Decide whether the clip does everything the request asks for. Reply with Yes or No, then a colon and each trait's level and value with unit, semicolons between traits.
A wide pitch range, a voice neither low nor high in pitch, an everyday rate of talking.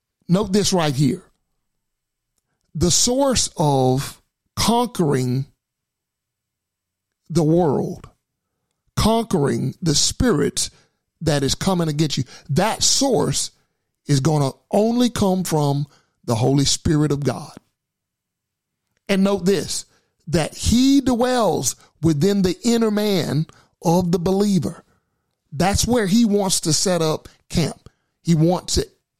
No: wide, 6.2 semitones; medium, 170 Hz; slow, 115 wpm